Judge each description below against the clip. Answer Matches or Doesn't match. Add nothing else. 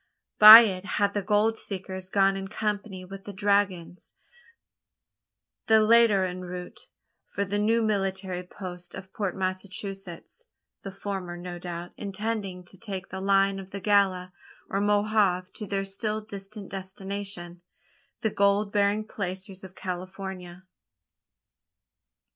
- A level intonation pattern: Matches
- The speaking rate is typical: Doesn't match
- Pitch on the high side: Matches